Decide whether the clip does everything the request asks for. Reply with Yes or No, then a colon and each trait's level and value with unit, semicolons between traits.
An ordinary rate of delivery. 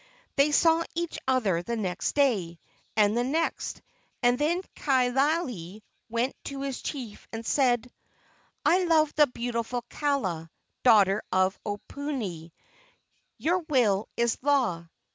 No: slow, 125 wpm